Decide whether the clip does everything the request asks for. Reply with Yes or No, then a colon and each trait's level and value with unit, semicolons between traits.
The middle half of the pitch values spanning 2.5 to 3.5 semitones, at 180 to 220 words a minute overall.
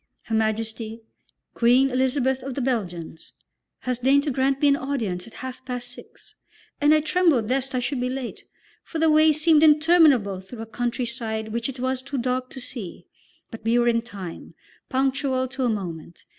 Yes: average, 3.2 semitones; average, 185 wpm